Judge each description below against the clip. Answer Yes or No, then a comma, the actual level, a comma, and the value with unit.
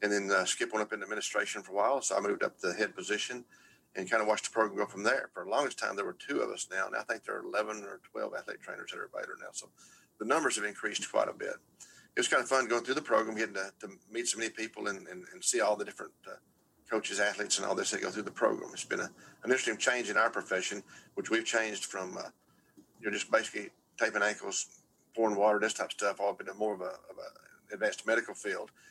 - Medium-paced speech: No, fast, 270 wpm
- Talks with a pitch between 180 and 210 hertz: No, low, 110 Hz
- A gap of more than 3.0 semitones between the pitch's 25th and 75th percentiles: No, narrow, 2.6 semitones